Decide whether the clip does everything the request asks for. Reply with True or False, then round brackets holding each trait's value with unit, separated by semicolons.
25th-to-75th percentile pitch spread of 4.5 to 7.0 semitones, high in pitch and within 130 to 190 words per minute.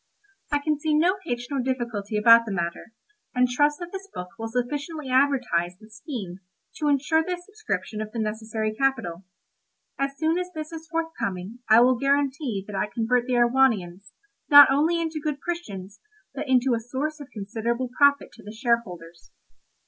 True (5.3 semitones; 250 Hz; 170 wpm)